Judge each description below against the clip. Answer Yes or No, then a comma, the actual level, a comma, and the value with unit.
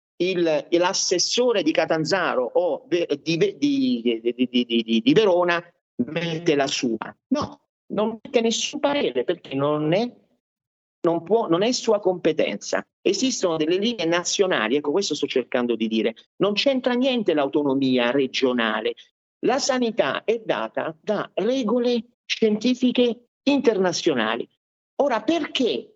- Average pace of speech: Yes, average, 125 wpm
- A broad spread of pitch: Yes, wide, 7.9 semitones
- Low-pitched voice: No, medium, 185 Hz